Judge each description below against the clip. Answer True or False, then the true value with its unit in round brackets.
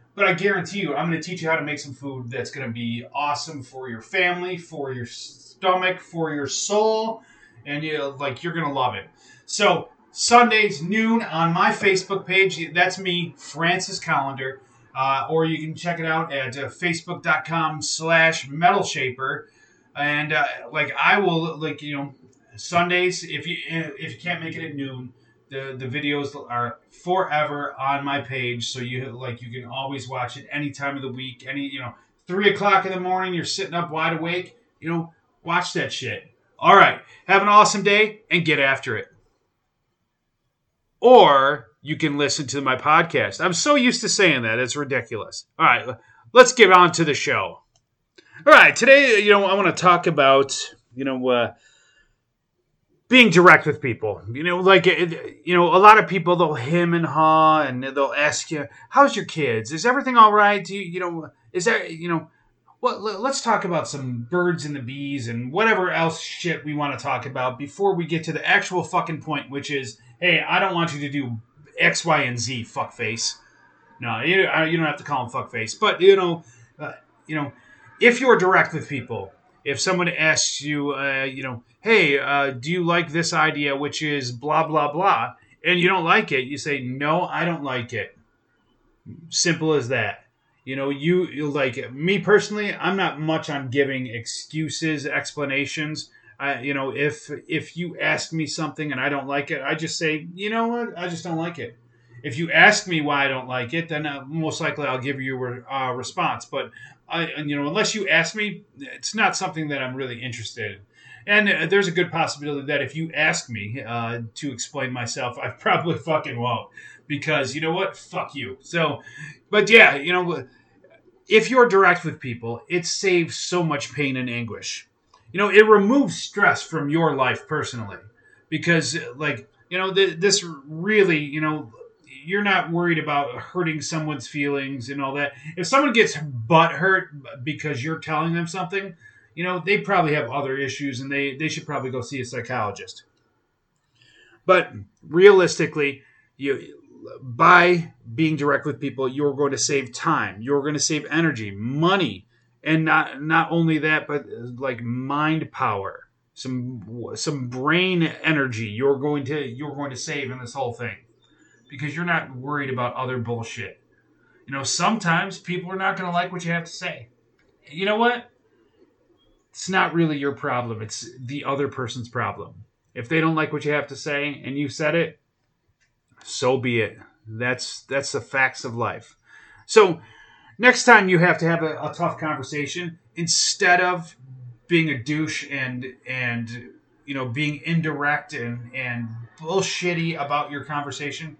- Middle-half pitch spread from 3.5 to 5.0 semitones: True (4.6 semitones)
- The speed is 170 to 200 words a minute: True (185 wpm)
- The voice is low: False (150 Hz)